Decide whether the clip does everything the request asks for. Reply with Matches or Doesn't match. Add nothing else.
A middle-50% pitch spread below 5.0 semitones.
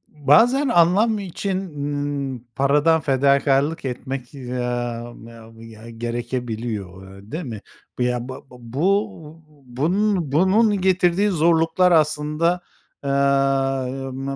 Doesn't match